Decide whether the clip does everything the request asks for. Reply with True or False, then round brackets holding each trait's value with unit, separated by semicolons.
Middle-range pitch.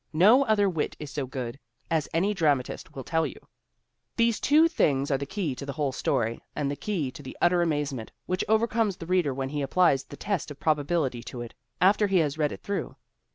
True (150 Hz)